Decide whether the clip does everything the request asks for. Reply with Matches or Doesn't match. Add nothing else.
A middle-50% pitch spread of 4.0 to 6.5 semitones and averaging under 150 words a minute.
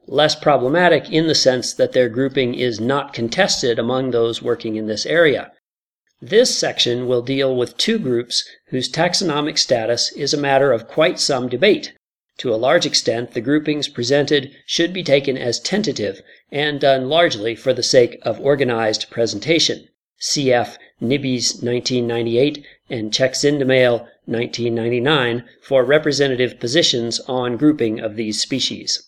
Doesn't match